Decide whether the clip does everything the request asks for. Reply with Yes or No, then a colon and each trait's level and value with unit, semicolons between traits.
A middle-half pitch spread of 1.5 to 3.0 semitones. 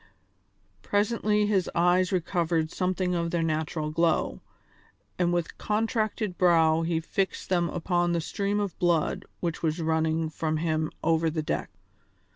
Yes: narrow, 2.4 semitones